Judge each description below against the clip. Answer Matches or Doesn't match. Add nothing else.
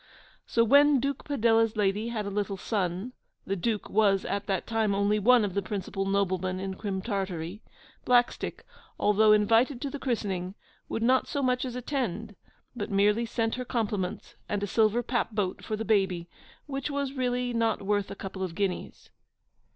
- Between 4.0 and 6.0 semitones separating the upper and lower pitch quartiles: Doesn't match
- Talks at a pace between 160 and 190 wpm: Matches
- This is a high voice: Matches